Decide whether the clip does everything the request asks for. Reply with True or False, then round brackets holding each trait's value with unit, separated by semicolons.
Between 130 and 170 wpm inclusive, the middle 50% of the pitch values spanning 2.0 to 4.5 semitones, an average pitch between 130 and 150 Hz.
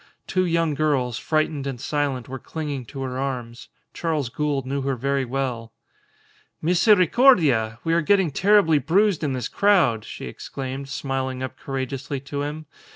True (155 wpm; 3.6 semitones; 140 Hz)